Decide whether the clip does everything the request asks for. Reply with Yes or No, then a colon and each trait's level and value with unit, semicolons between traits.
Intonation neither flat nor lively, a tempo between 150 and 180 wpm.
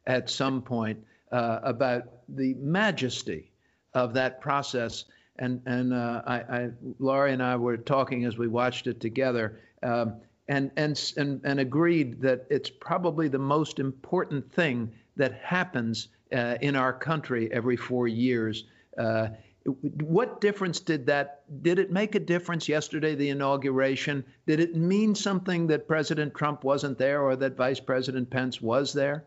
Yes: average, 3.5 semitones; average, 155 wpm